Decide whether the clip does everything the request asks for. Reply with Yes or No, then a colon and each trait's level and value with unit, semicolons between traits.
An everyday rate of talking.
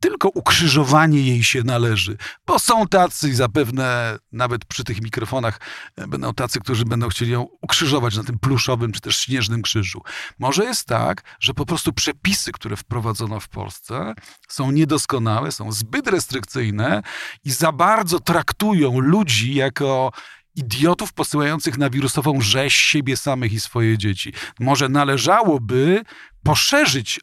Yes: average, 135 wpm